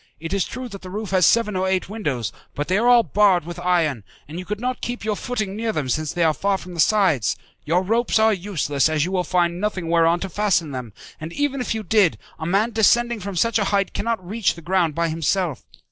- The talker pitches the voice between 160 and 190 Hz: Yes, medium, 185 Hz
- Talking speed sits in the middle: No, fast, 245 wpm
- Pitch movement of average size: Yes, average, 4.4 semitones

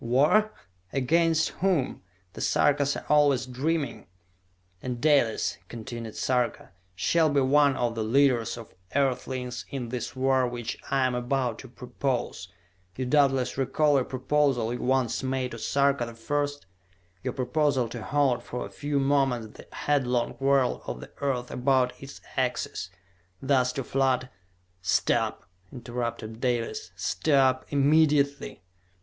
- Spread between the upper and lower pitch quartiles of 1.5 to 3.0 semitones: Yes, narrow, 2.5 semitones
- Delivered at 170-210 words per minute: No, average, 140 wpm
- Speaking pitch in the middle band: No, low, 130 Hz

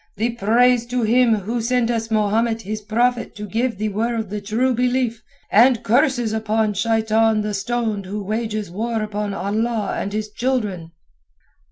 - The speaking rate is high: No, average, 160 wpm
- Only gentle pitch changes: Yes, narrow, 2.1 semitones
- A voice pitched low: No, high, 220 Hz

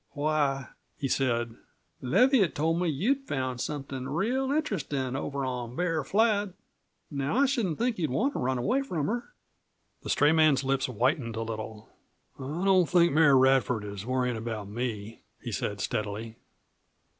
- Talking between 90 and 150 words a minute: No, average, 160 wpm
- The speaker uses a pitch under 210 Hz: Yes, medium, 140 Hz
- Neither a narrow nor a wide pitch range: No, wide, 6.5 semitones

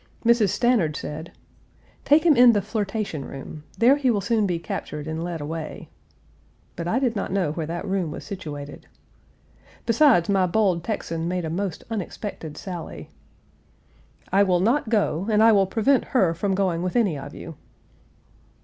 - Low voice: No, high, 190 Hz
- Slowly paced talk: No, average, 165 wpm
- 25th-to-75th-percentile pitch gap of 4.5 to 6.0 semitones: Yes, average, 5.1 semitones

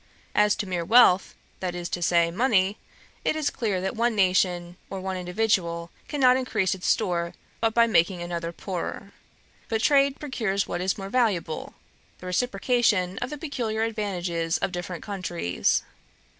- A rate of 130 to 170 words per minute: Yes, average, 155 wpm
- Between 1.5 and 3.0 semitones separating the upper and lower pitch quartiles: No, average, 4.2 semitones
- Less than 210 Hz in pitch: Yes, high, 190 Hz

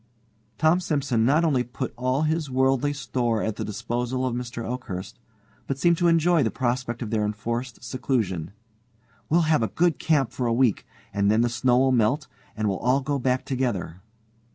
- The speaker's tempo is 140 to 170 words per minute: No, average, 180 wpm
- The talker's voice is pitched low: Yes, low, 125 Hz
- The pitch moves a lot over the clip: No, average, 3.4 semitones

